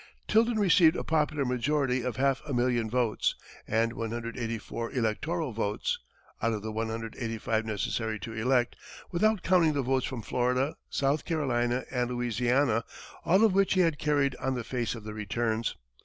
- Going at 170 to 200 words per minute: No, average, 160 wpm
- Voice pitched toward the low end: Yes, low, 125 Hz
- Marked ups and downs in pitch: No, average, 4.3 semitones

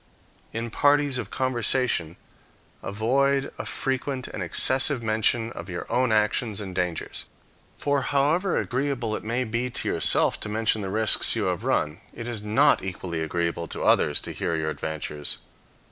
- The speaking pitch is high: No, low, 115 Hz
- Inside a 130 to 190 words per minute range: Yes, average, 160 wpm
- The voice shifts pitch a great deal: Yes, wide, 5.7 semitones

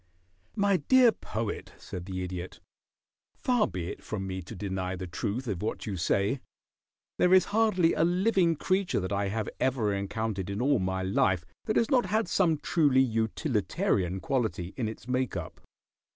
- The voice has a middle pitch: No, low, 110 Hz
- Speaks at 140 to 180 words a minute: Yes, average, 170 wpm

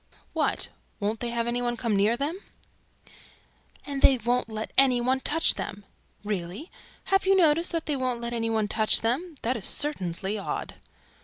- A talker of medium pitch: No, high, 240 Hz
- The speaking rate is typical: Yes, average, 175 wpm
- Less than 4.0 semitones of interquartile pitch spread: No, average, 4.7 semitones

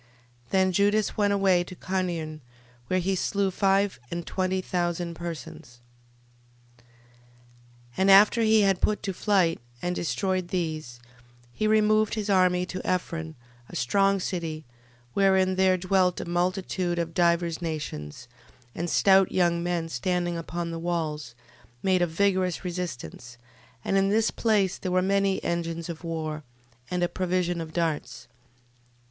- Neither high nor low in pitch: Yes, medium, 180 Hz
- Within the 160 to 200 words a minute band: No, average, 145 wpm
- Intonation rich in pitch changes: No, narrow, 2.5 semitones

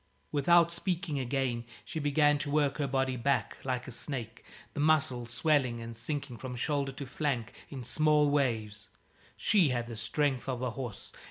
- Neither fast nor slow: Yes, average, 170 wpm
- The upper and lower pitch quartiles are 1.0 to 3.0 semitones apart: No, average, 3.4 semitones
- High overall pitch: No, low, 135 Hz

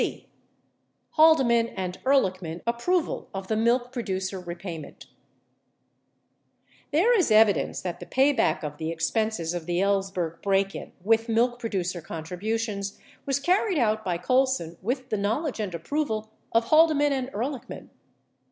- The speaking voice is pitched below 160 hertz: No, high, 220 Hz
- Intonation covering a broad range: Yes, wide, 5.9 semitones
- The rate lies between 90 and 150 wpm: Yes, average, 145 wpm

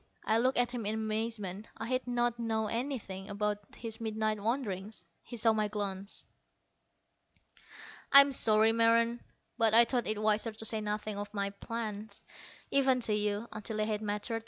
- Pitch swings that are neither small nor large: No, narrow, 1.8 semitones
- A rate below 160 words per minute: No, average, 165 wpm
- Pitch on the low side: No, high, 220 Hz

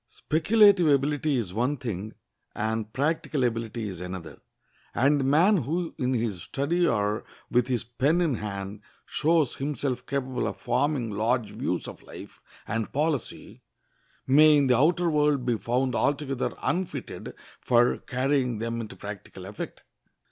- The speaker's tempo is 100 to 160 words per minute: Yes, average, 145 wpm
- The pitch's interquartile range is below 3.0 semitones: No, average, 4.9 semitones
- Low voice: Yes, low, 130 Hz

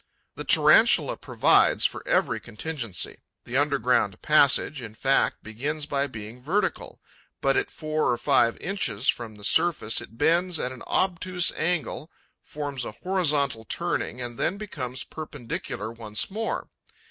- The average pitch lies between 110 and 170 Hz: Yes, medium, 140 Hz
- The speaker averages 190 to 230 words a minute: No, average, 140 wpm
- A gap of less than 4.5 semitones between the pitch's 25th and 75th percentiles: No, wide, 5.6 semitones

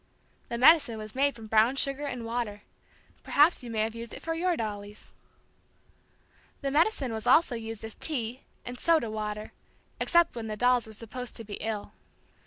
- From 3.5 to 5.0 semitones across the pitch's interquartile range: Yes, average, 4.1 semitones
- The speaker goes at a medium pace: Yes, average, 180 wpm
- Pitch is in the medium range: No, high, 235 Hz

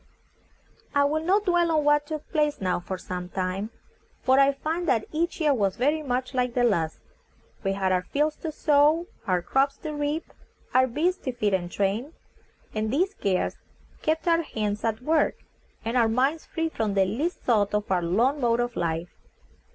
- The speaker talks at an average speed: Yes, average, 190 wpm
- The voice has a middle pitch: No, very high, 255 Hz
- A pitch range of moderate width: No, wide, 7.1 semitones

